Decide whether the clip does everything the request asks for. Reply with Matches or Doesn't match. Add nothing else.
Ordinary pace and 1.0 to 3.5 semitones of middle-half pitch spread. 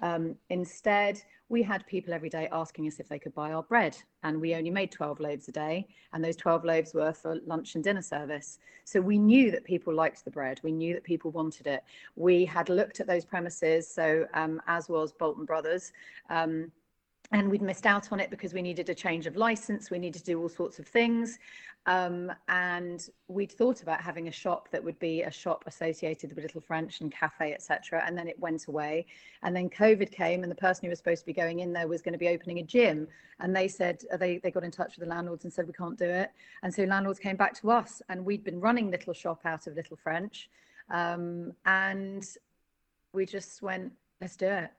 Doesn't match